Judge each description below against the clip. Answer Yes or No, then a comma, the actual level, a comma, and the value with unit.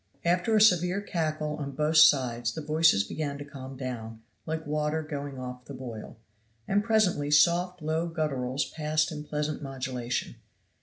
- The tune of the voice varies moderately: Yes, average, 3.4 semitones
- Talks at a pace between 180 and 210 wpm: No, average, 155 wpm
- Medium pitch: Yes, medium, 150 Hz